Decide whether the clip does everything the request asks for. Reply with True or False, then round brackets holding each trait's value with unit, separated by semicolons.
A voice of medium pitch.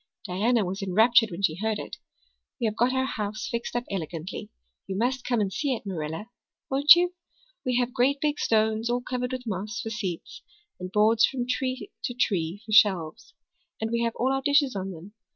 False (225 Hz)